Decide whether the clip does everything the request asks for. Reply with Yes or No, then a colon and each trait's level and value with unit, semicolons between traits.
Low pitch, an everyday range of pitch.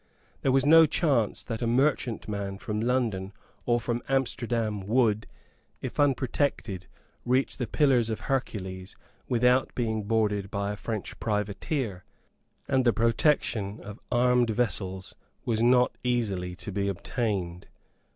Yes: low, 115 Hz; average, 3.7 semitones